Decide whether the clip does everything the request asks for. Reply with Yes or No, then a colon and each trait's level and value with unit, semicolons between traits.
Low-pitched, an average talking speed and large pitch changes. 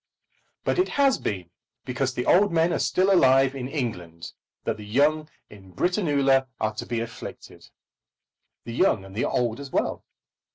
Yes: low, 130 Hz; average, 165 wpm; wide, 6.3 semitones